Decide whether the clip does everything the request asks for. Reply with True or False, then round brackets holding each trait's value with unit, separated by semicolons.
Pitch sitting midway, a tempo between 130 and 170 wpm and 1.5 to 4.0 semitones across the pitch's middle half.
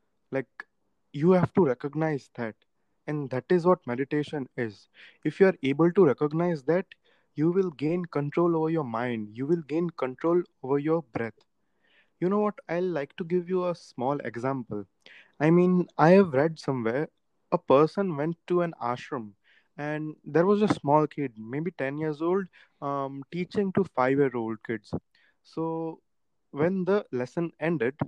False (155 Hz; 165 wpm; 4.5 semitones)